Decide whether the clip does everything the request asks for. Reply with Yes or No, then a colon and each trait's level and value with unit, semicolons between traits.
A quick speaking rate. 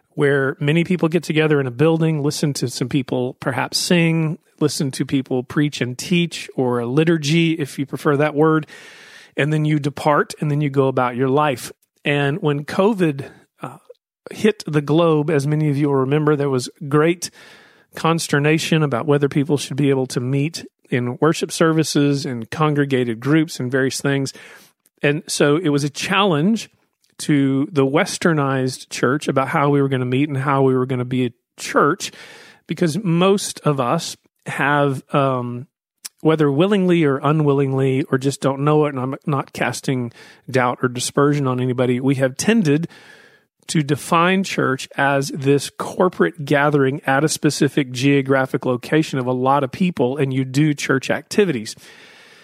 No: average, 170 wpm